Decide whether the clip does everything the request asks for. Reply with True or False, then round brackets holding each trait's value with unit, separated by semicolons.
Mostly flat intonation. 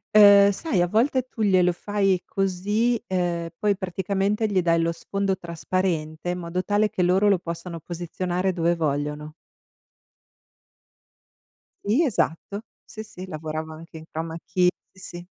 False (3.1 semitones)